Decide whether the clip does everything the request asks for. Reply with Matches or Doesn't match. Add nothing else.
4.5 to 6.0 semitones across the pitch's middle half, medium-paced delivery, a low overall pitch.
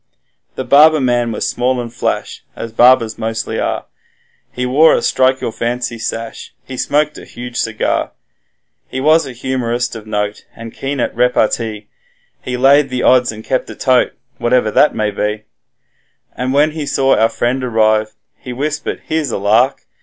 Doesn't match